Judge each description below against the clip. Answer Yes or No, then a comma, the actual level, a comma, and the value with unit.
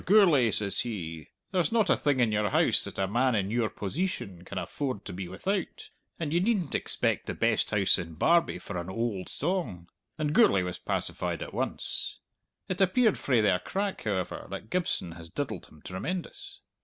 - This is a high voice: No, low, 115 Hz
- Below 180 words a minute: No, average, 185 wpm